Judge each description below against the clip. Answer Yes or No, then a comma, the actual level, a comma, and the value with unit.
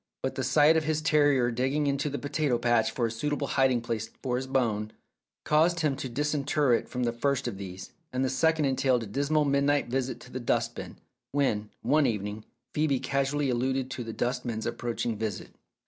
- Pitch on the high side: No, low, 130 Hz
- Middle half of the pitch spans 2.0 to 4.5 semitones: Yes, average, 3.4 semitones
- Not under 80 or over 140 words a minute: No, average, 200 wpm